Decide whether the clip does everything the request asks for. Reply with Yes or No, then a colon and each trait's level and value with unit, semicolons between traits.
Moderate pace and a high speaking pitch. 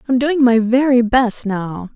Yes: average, 185 wpm; high, 240 Hz